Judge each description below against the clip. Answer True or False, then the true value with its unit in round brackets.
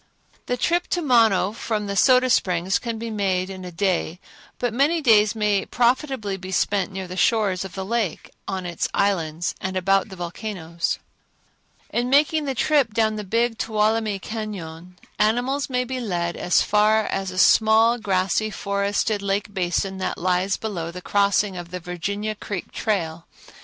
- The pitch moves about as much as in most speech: True (3.5 semitones)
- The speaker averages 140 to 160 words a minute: False (170 wpm)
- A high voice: True (205 Hz)